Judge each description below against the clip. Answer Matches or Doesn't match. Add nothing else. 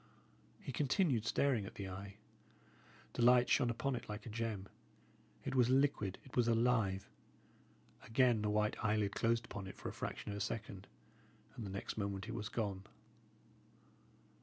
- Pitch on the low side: Matches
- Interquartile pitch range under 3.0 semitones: Doesn't match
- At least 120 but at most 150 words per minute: Doesn't match